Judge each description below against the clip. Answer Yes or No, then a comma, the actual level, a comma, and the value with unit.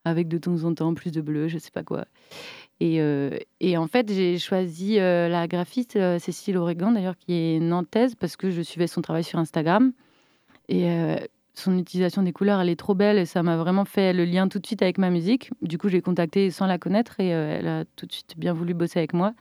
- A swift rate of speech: Yes, fast, 240 wpm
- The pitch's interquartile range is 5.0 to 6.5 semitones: No, average, 2.7 semitones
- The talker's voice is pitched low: No, medium, 180 Hz